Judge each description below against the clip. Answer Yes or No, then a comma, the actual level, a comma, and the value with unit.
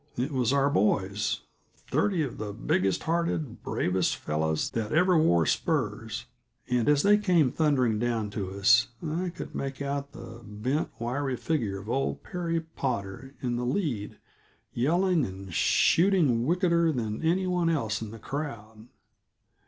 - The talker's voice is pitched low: Yes, low, 130 Hz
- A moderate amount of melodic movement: No, wide, 6.9 semitones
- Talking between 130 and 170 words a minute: Yes, average, 150 wpm